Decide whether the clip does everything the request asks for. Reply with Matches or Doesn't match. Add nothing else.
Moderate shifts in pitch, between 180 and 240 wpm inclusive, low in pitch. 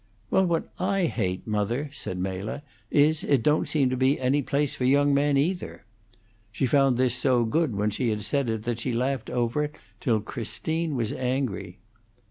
Matches